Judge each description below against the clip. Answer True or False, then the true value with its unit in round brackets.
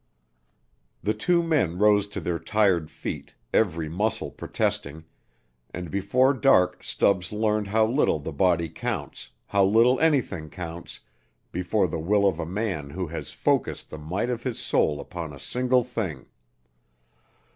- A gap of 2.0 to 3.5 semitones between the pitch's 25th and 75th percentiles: False (5.2 semitones)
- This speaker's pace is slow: False (145 wpm)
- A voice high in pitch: False (95 Hz)